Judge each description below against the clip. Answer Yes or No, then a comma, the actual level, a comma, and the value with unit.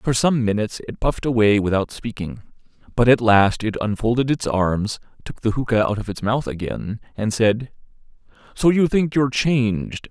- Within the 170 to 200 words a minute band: Yes, average, 190 wpm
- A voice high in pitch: No, low, 115 Hz